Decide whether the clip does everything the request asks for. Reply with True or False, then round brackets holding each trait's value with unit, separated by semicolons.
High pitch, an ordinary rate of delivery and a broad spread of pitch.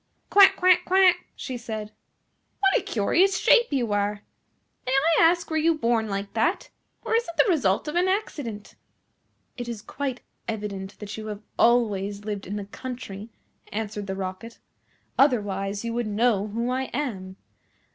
True (230 Hz; 165 wpm; 6.5 semitones)